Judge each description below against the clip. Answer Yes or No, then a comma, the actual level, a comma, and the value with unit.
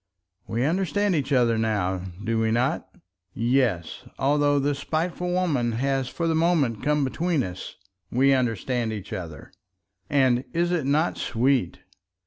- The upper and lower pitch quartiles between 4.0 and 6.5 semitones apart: Yes, average, 5.1 semitones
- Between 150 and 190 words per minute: No, average, 140 wpm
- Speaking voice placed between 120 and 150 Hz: Yes, low, 135 Hz